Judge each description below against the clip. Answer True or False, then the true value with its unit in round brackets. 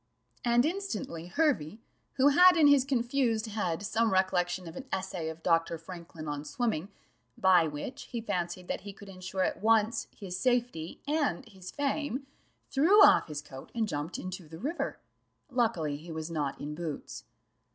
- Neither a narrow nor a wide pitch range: False (6.9 semitones)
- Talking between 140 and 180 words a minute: True (170 wpm)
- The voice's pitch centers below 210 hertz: True (190 Hz)